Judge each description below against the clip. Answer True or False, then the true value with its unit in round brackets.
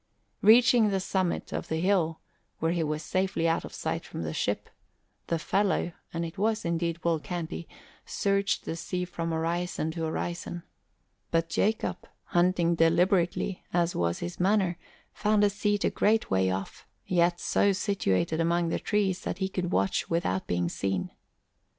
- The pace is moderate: True (165 wpm)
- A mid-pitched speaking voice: True (175 Hz)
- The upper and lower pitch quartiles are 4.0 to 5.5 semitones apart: False (2.8 semitones)